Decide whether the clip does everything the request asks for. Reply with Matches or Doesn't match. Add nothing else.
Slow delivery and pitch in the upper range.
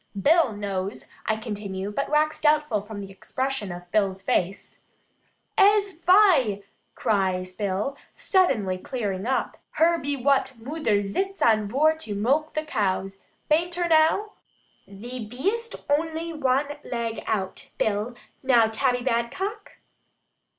Matches